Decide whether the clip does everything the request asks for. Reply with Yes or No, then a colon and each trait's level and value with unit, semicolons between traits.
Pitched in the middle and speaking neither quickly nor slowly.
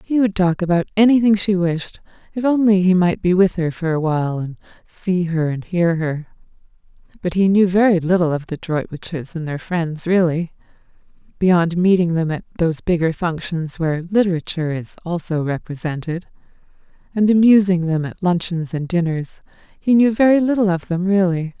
Yes: medium, 175 Hz; average, 165 wpm